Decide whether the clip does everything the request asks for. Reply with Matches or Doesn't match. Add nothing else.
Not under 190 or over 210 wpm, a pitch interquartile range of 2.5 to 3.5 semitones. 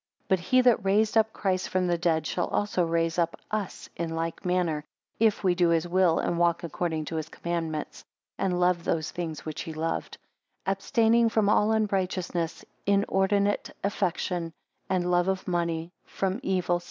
Doesn't match